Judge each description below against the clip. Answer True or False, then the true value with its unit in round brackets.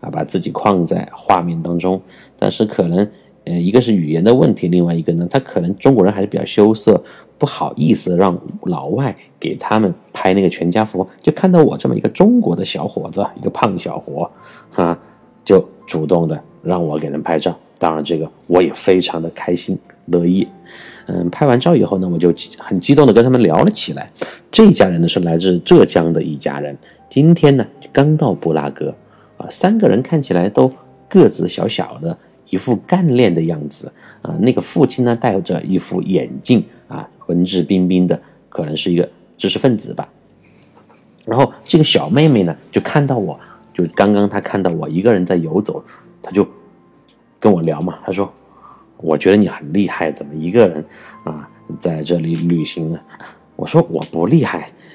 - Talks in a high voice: False (90 Hz)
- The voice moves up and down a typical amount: False (5.9 semitones)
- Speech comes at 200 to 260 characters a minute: False (270 characters per minute)